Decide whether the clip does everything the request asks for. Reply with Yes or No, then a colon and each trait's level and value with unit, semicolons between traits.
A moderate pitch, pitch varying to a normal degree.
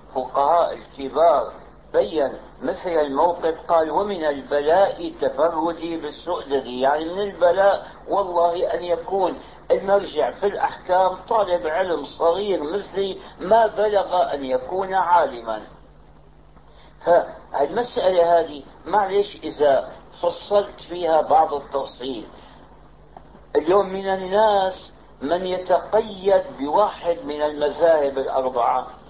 Yes: medium, 175 Hz; average, 5.0 semitones